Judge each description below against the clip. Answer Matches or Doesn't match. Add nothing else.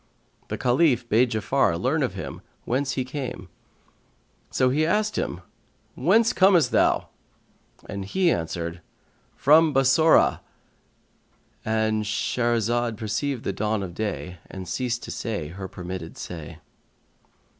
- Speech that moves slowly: Matches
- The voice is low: Matches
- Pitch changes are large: Matches